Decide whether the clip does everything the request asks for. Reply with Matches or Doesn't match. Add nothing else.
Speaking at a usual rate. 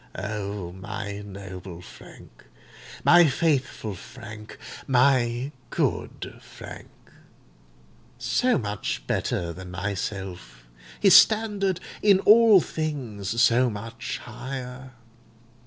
Doesn't match